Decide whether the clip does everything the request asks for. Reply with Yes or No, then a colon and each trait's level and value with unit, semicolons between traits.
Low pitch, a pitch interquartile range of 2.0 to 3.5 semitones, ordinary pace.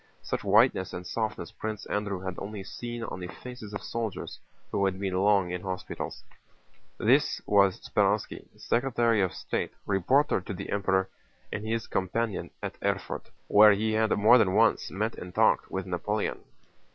Yes: low, 105 Hz; average, 2.7 semitones; average, 165 wpm